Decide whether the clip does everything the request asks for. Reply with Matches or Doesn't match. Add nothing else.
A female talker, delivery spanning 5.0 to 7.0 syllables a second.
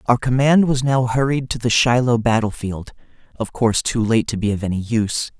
Doesn't match